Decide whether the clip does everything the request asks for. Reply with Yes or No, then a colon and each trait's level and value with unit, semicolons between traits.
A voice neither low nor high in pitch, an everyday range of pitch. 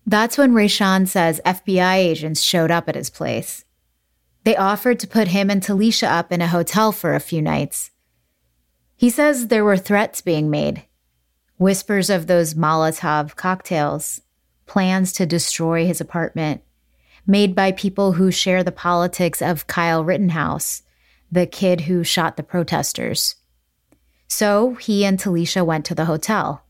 Yes: medium, 175 Hz; average, 3.9 semitones